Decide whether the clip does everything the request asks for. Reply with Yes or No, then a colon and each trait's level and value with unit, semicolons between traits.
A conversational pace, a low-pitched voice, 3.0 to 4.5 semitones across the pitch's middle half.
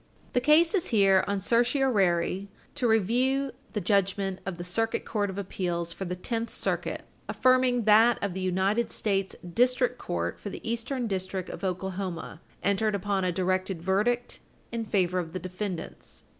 No: average, 160 wpm; high, 200 Hz; average, 4.0 semitones